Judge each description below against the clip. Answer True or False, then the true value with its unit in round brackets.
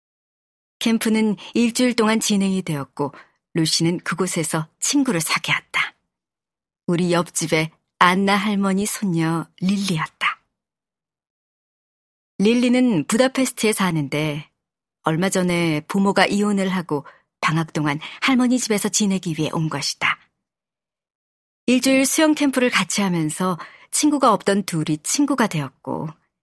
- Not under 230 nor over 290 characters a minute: True (255 characters per minute)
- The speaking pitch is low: False (190 Hz)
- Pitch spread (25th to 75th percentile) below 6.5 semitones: True (5.6 semitones)